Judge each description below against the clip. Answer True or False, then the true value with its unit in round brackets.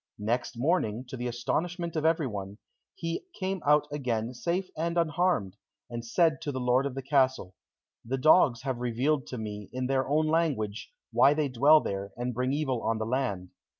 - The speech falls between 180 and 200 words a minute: True (185 wpm)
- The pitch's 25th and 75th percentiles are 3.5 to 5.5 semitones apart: True (4.7 semitones)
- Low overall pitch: True (130 Hz)